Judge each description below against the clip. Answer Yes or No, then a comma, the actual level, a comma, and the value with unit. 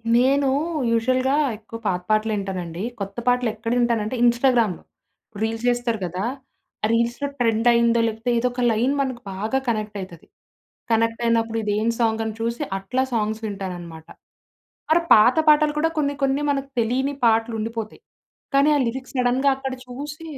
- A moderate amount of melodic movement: Yes, average, 3.0 semitones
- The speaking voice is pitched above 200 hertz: Yes, high, 230 Hz